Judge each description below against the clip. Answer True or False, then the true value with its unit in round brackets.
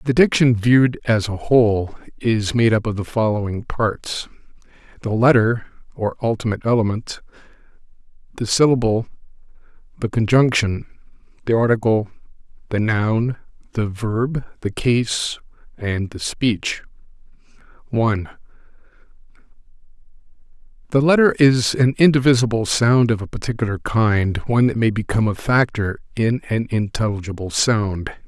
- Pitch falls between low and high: False (115 Hz)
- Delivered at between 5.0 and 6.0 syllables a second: False (4.5 syllables/s)